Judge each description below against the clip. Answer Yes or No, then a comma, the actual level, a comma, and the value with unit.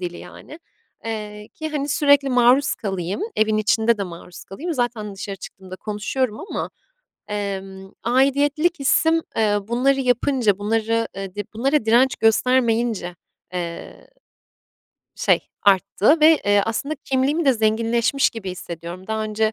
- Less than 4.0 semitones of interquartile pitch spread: No, average, 4.7 semitones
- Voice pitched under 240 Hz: Yes, high, 225 Hz